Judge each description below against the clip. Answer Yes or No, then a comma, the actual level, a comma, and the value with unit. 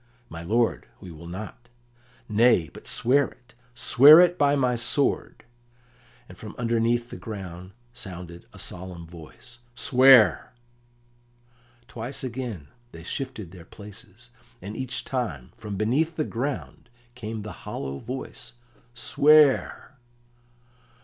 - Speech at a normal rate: No, slow, 115 wpm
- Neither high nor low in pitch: No, low, 115 Hz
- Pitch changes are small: No, wide, 5.6 semitones